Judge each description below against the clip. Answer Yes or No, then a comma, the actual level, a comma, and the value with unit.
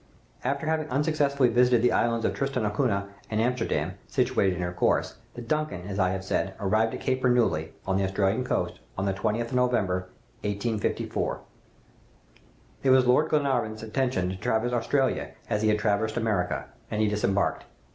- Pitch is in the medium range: No, low, 110 Hz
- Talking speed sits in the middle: Yes, average, 170 wpm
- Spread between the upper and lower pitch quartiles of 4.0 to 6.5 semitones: Yes, average, 4.3 semitones